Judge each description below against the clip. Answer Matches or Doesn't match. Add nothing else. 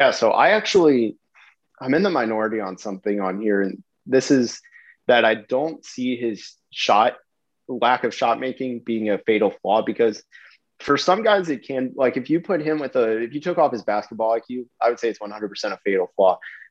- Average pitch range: Matches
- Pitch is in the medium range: Doesn't match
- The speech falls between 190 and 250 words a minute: Matches